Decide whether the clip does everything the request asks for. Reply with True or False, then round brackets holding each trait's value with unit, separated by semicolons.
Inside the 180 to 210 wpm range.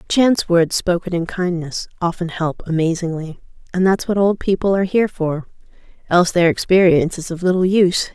False (160 wpm)